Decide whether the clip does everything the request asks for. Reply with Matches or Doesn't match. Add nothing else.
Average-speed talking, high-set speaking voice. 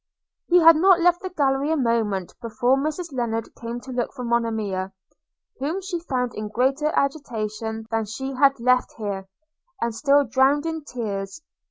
Matches